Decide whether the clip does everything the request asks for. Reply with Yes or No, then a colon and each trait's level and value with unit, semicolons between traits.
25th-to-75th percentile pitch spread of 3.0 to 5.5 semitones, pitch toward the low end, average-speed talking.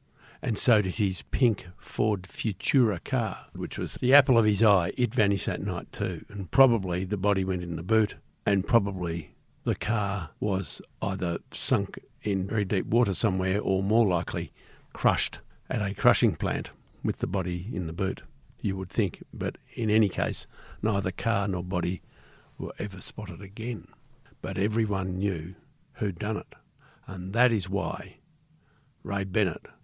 Yes: average, 3.7 semitones; low, 100 Hz; average, 165 wpm